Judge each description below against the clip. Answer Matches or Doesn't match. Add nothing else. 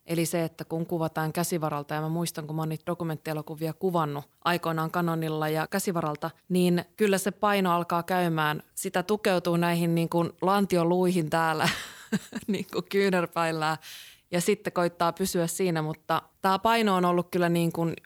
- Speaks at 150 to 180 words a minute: Matches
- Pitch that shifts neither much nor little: Doesn't match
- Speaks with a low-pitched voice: Doesn't match